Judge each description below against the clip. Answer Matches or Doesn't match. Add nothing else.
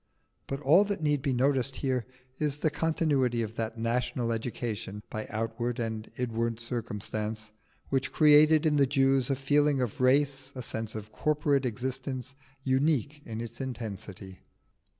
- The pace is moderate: Matches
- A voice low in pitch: Matches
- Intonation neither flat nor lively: Matches